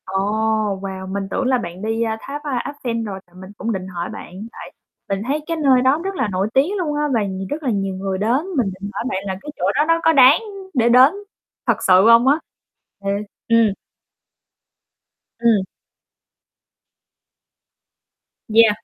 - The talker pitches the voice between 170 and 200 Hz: No, high, 230 Hz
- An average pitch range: No, wide, 5.7 semitones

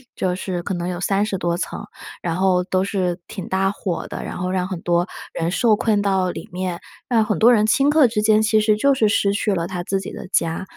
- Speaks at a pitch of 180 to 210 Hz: Yes, high, 190 Hz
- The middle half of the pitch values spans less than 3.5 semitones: Yes, average, 2.9 semitones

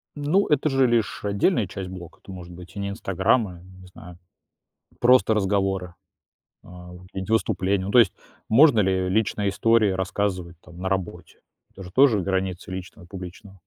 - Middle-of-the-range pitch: No, very low, 95 Hz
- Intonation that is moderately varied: Yes, average, 3.0 semitones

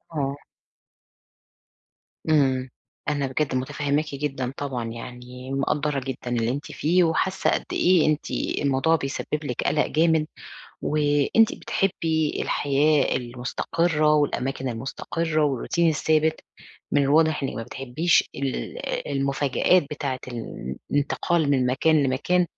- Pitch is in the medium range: Yes, medium, 145 Hz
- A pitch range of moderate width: Yes, average, 3.1 semitones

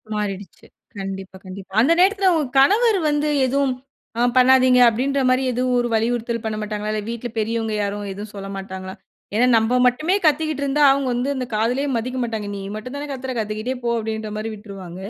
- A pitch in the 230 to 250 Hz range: Yes, high, 235 Hz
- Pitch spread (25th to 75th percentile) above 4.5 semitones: No, average, 3.9 semitones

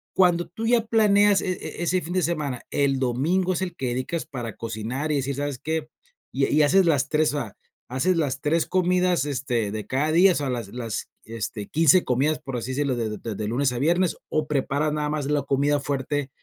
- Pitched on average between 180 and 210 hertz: No, medium, 145 Hz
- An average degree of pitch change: Yes, average, 4.8 semitones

